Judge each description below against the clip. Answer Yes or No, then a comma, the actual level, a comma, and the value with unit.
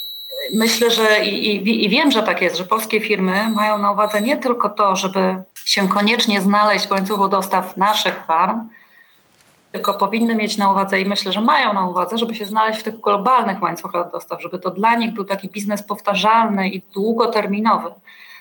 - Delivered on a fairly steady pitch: Yes, narrow, 2.2 semitones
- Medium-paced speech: No, fast, 185 wpm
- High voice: Yes, high, 205 Hz